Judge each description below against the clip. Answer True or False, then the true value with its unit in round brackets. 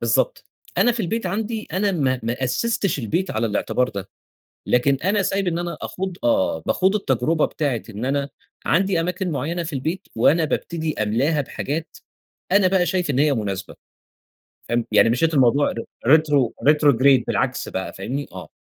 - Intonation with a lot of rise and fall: True (6.4 semitones)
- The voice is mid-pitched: True (155 Hz)